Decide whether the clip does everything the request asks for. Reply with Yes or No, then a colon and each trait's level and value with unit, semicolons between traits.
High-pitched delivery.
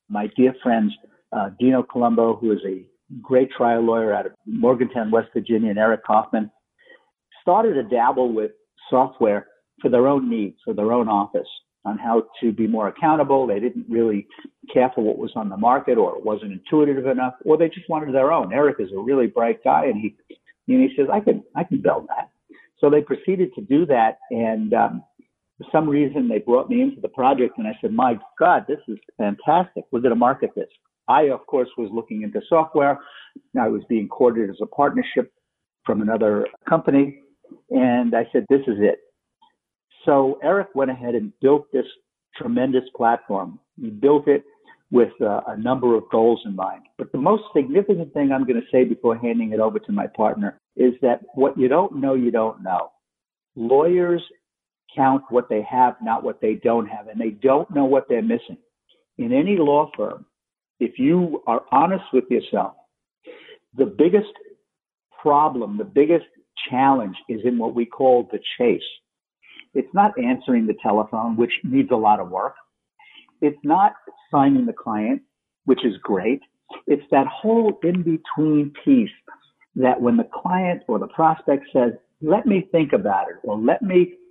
No: medium, 140 Hz